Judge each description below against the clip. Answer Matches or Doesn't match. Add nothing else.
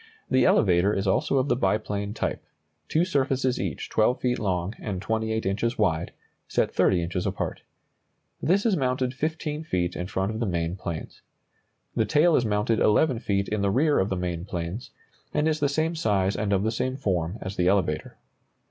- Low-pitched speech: Matches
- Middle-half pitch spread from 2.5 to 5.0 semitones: Doesn't match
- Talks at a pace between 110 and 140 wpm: Doesn't match